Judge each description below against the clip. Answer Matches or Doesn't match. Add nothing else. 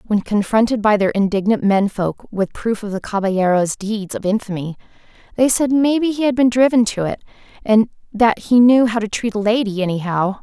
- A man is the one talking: Doesn't match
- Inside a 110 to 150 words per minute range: Doesn't match